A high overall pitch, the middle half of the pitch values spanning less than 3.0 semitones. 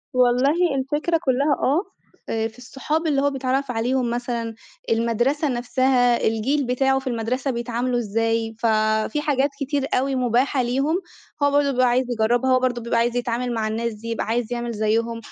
Yes: very high, 250 Hz; narrow, 2.6 semitones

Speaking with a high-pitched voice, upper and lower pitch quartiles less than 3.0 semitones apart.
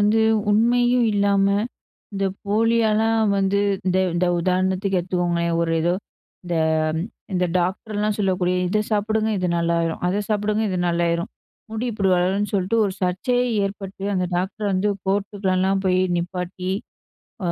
Yes: high, 195 Hz; narrow, 2.5 semitones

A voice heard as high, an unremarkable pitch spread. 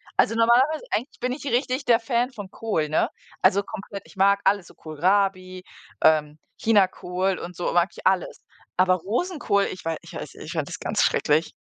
Yes: high, 195 Hz; average, 4.3 semitones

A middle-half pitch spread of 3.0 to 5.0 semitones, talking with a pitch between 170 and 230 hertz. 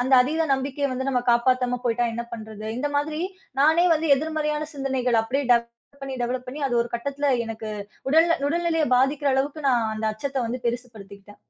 No: average, 3.7 semitones; very high, 265 Hz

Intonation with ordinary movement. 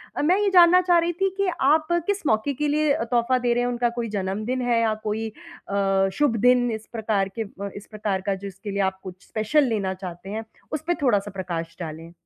No: wide, 6.6 semitones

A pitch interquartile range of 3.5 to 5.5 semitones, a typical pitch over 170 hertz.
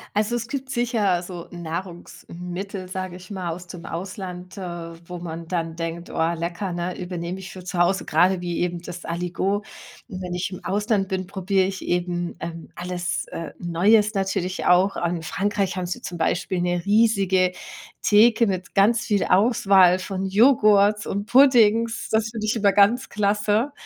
No: average, 2.8 semitones; medium, 185 Hz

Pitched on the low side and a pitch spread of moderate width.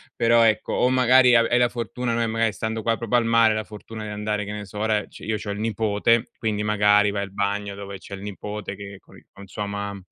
No: low, 105 Hz; narrow, 2.1 semitones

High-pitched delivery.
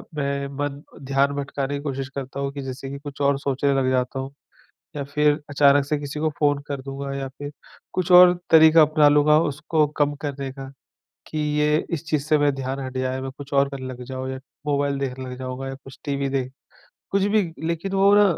No: medium, 140 Hz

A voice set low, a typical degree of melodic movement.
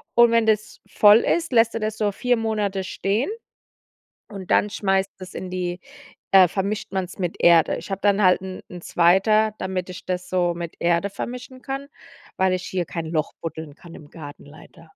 No: high, 190 Hz; average, 3.4 semitones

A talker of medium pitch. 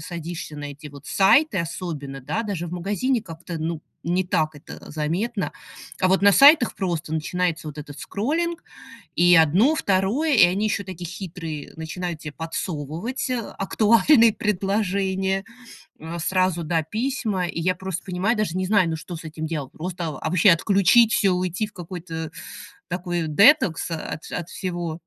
Yes: medium, 180 Hz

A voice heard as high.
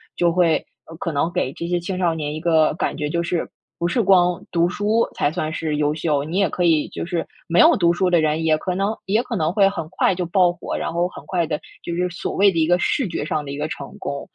No: medium, 170 Hz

